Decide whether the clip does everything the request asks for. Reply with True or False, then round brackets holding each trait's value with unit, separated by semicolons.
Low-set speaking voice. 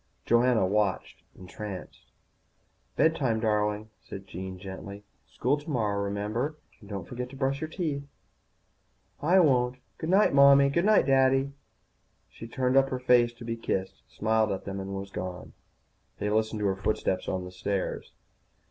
True (115 Hz)